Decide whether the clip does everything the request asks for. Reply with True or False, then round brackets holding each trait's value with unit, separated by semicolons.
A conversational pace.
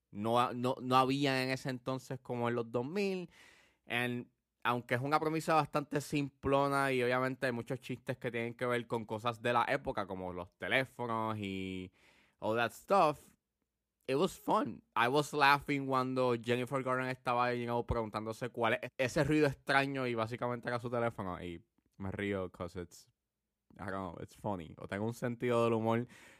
True (180 wpm)